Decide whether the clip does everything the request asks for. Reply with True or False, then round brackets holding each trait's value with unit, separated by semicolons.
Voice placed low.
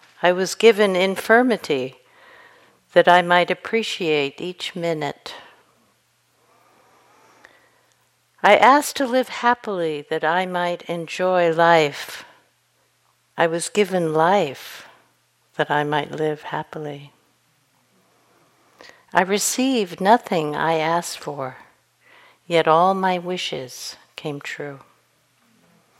False (175 Hz)